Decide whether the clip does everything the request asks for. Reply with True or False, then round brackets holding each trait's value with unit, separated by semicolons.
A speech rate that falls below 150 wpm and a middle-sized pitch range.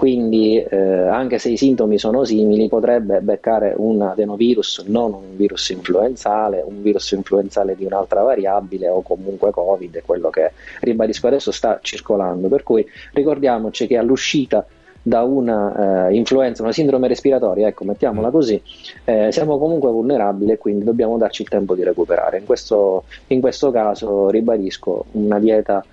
False (155 wpm; 3.9 semitones)